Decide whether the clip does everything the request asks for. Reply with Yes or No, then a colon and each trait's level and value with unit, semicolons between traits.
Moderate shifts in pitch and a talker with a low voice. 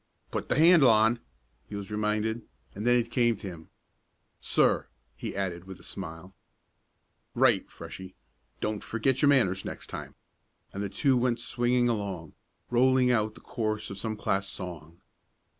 Yes: average, 4.0 semitones; low, 110 Hz